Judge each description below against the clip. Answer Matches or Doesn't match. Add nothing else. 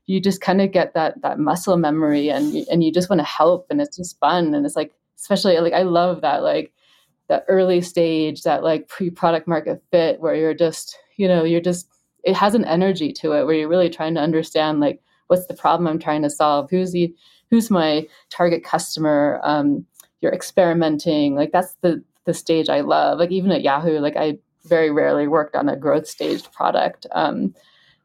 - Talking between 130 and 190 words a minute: Doesn't match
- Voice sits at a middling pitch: Matches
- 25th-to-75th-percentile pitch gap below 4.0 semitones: Matches